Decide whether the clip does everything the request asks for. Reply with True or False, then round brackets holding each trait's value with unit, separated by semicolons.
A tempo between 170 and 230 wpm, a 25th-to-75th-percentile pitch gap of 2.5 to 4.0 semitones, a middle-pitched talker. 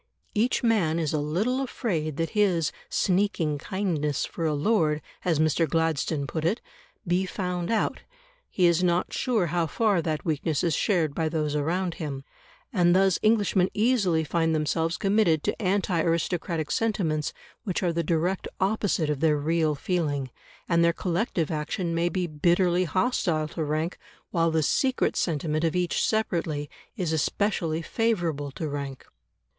False (155 wpm; 3.3 semitones; 170 Hz)